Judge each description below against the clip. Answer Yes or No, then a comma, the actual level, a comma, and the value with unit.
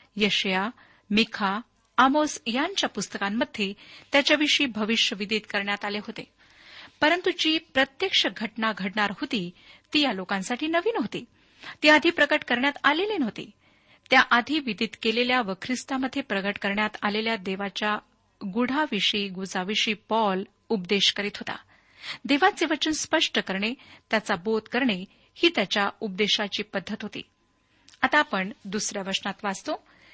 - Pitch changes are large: Yes, wide, 5.7 semitones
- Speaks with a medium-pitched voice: No, high, 225 Hz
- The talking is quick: No, average, 115 wpm